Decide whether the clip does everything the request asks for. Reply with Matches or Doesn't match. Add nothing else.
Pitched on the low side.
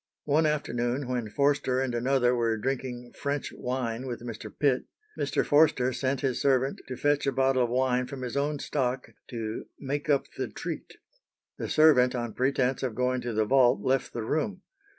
Matches